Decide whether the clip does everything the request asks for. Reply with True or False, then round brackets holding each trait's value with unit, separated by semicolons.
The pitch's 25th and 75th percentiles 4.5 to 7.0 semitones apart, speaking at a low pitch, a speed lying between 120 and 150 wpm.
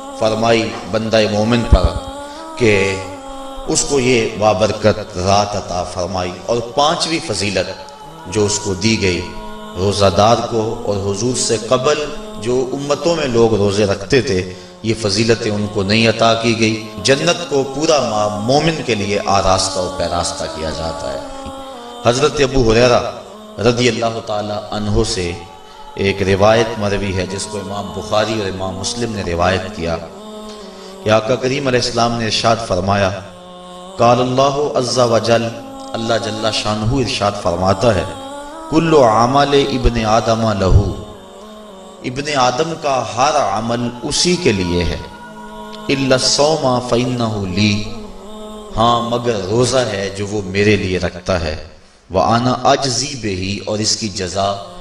True (4.9 semitones; 115 Hz; 140 wpm)